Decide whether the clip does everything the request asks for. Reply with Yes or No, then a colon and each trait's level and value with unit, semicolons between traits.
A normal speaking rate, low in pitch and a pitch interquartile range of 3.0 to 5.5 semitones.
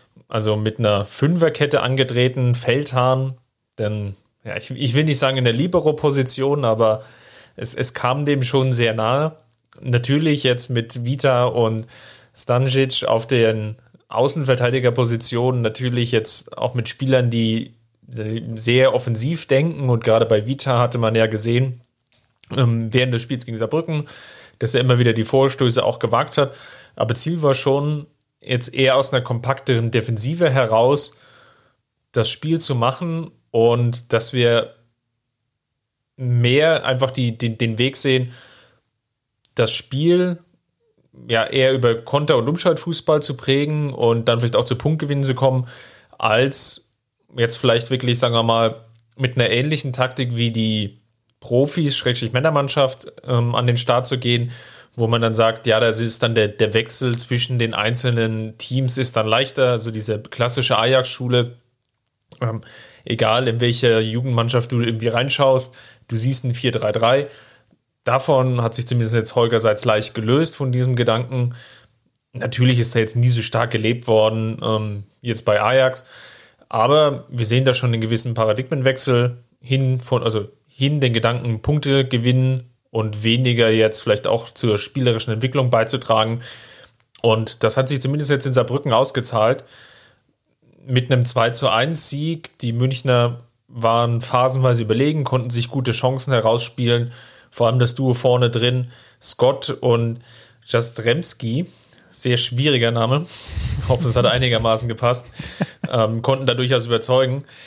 No: average, 145 wpm; low, 125 Hz; narrow, 2.5 semitones